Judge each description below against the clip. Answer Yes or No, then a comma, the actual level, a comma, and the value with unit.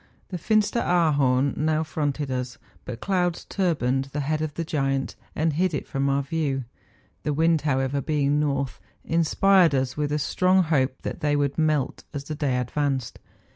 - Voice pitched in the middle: Yes, medium, 145 Hz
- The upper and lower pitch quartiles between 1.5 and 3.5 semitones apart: Yes, average, 2.9 semitones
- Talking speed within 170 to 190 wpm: Yes, average, 175 wpm